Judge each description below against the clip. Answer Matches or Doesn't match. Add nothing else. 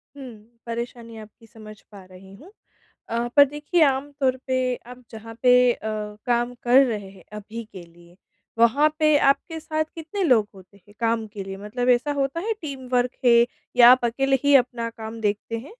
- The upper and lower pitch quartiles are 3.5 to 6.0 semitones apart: Matches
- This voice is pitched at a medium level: Doesn't match